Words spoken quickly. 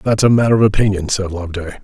Yes: fast, 230 wpm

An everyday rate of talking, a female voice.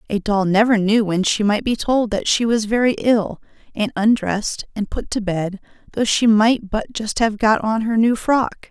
No: fast, 215 wpm; female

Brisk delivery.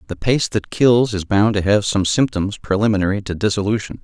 No: average, 195 wpm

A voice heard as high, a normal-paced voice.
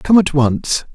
No: medium, 155 Hz; average, 190 wpm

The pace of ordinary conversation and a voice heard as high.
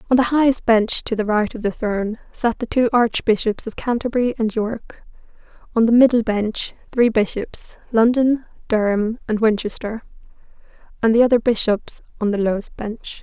Yes: average, 165 wpm; high, 225 Hz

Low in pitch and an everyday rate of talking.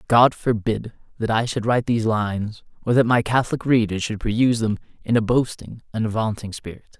Yes: low, 115 Hz; average, 190 wpm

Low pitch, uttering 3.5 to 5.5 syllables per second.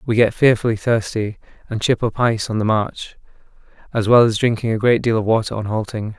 No: low, 110 Hz; 5.8 syllables/s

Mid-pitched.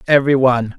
No: low, 130 Hz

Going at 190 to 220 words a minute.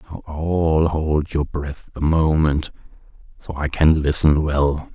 No: average, 145 wpm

